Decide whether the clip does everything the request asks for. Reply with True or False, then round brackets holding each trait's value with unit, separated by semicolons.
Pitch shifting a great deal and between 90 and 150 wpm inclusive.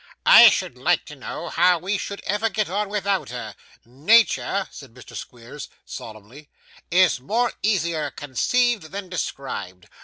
True (7.7 semitones; 145 wpm)